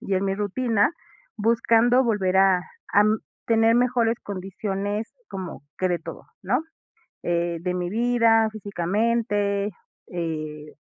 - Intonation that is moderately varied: Yes, average, 3.6 semitones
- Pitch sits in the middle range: No, high, 205 Hz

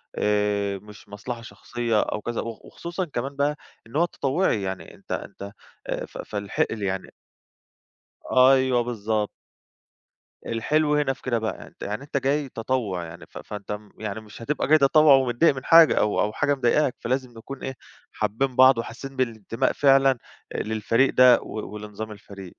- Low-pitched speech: Yes, low, 120 Hz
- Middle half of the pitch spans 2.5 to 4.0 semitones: No, average, 4.4 semitones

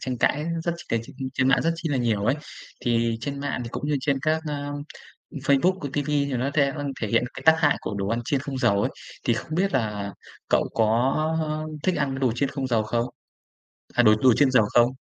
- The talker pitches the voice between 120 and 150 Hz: Yes, low, 135 Hz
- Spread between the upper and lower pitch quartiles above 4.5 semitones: No, average, 3.9 semitones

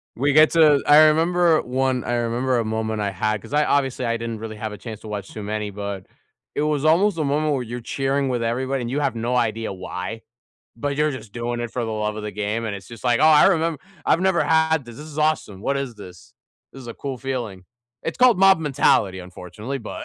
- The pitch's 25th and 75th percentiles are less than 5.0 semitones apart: No, average, 5.3 semitones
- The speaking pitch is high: No, low, 125 Hz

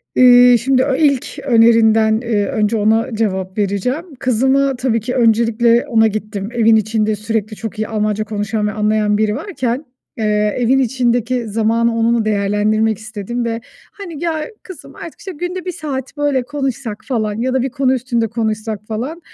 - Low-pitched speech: No, high, 230 Hz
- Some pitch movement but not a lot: Yes, average, 3.2 semitones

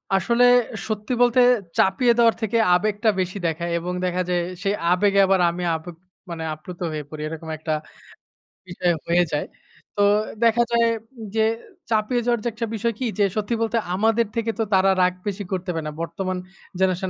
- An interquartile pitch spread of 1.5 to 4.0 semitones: No, average, 4.4 semitones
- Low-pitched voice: No, high, 195 Hz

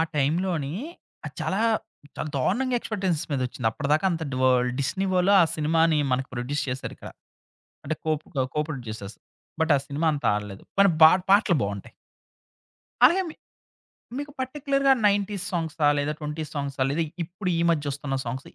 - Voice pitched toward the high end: No, medium, 155 Hz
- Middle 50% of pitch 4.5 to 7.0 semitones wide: Yes, wide, 5.6 semitones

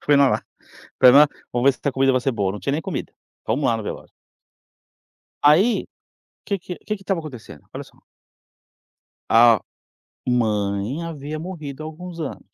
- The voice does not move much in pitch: No, average, 5.2 semitones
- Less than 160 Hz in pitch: Yes, medium, 140 Hz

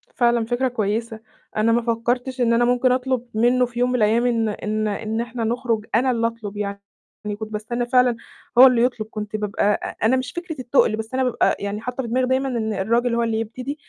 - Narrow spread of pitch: Yes, narrow, 2.3 semitones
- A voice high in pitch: Yes, high, 235 Hz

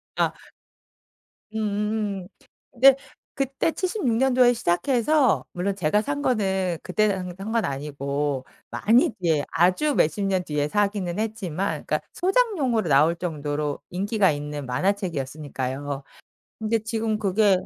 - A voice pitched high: Yes, high, 195 Hz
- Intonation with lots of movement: Yes, wide, 6.4 semitones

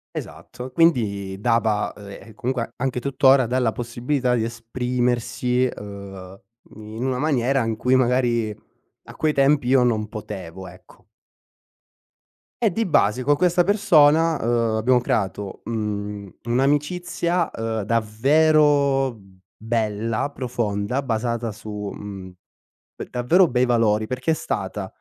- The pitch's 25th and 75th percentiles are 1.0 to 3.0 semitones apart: No, average, 4.0 semitones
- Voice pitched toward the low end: Yes, low, 120 Hz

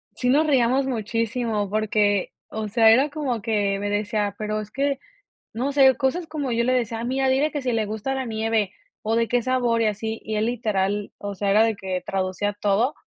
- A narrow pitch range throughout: No, average, 3.7 semitones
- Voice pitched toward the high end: Yes, high, 225 Hz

